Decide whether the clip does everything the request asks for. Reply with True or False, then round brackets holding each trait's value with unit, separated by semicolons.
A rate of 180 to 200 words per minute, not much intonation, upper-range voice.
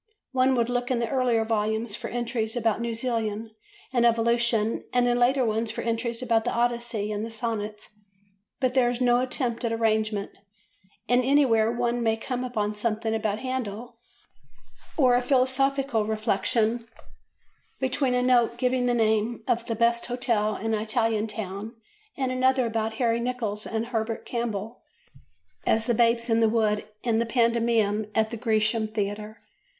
False (165 wpm; 1.9 semitones; 230 Hz)